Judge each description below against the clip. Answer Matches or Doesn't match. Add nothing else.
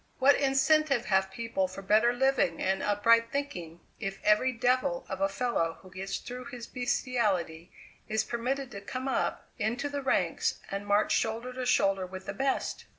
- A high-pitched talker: Matches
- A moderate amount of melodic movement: Matches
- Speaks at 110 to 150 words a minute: Doesn't match